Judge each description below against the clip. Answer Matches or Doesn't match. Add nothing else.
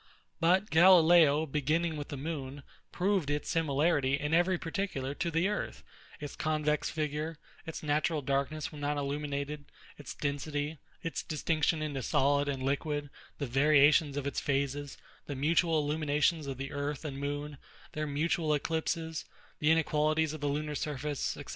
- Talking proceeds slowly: Doesn't match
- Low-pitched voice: Doesn't match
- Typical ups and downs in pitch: Doesn't match